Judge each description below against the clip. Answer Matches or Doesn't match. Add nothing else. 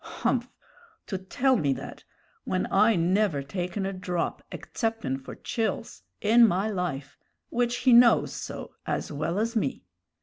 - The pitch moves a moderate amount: Matches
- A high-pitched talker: Matches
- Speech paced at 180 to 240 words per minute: Doesn't match